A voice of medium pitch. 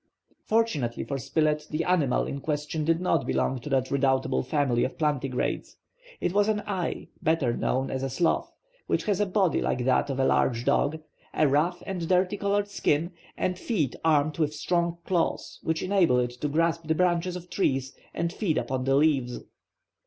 Yes: medium, 155 Hz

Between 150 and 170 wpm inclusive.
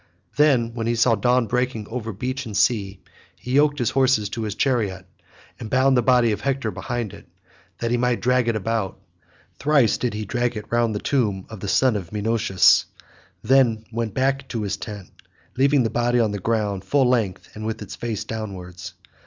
No: average, 200 wpm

